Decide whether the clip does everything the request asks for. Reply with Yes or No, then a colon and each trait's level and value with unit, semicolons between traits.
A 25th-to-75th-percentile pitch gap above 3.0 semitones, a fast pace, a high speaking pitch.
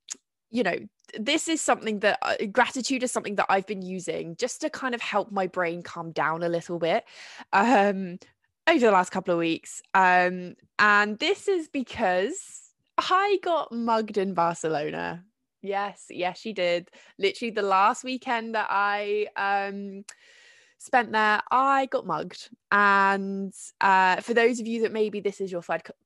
No: average, 5.1 semitones; average, 165 wpm; high, 205 Hz